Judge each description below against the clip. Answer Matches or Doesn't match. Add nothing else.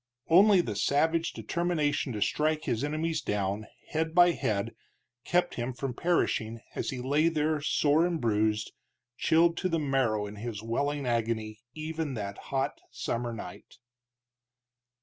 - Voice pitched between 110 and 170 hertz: Matches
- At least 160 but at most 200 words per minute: Doesn't match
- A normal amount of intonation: Doesn't match